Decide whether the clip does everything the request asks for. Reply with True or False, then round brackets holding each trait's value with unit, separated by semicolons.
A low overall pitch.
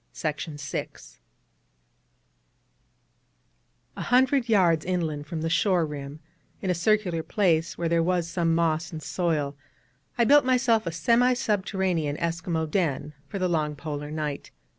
False (170 Hz)